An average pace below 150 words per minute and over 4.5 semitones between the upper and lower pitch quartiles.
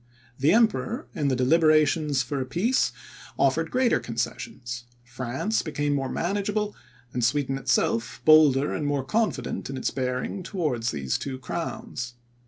Yes: average, 140 wpm; wide, 5.4 semitones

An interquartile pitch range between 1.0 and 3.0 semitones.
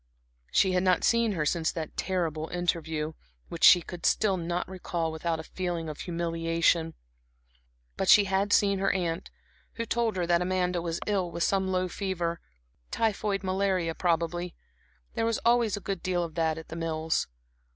Yes: narrow, 2.5 semitones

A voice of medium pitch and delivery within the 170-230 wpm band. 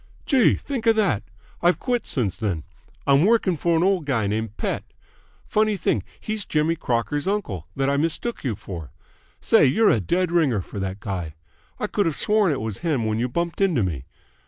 Yes: medium, 145 Hz; average, 195 wpm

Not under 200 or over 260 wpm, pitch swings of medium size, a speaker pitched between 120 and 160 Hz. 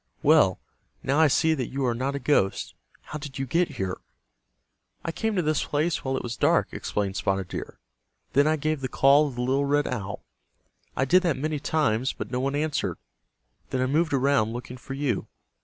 Yes: fast, 205 wpm; average, 3.4 semitones; low, 135 Hz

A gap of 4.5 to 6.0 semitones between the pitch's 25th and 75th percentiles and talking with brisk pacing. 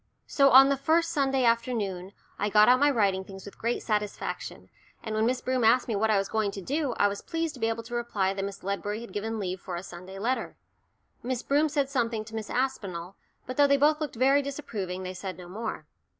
Yes: average, 5.1 semitones; fast, 235 wpm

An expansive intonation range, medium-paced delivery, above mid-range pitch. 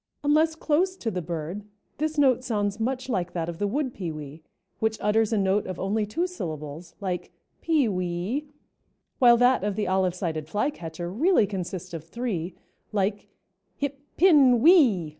Yes: wide, 6.6 semitones; average, 160 wpm; high, 205 Hz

